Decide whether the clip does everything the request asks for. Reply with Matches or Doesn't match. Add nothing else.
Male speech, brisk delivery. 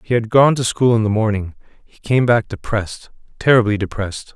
Doesn't match